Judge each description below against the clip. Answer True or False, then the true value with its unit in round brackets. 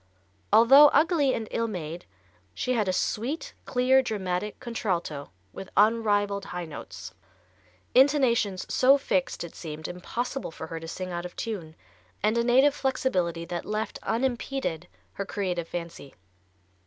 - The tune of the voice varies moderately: False (6.2 semitones)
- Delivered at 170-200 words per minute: False (140 wpm)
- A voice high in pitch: True (210 Hz)